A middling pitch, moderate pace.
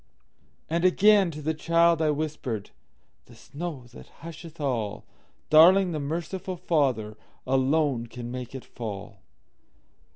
No: medium, 155 Hz; slow, 105 wpm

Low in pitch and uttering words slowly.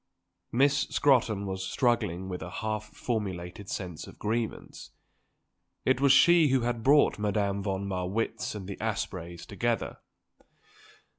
Yes: low, 105 Hz; slow, 130 wpm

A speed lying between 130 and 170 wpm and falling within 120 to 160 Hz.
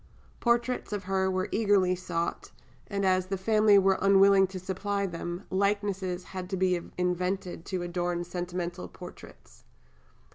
No: average, 140 wpm; high, 190 Hz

